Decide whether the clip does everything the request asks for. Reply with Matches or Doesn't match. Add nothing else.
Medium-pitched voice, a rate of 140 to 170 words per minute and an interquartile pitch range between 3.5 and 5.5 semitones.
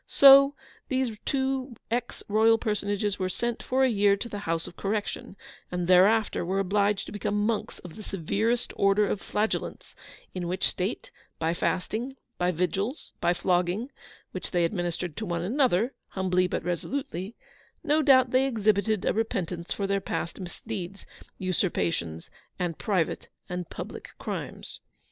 Doesn't match